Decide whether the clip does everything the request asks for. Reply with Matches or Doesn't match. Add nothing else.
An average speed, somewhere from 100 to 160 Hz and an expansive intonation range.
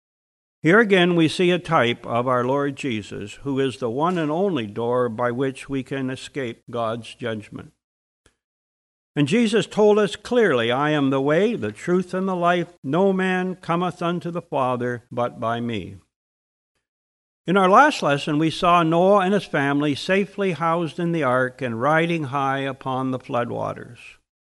Matches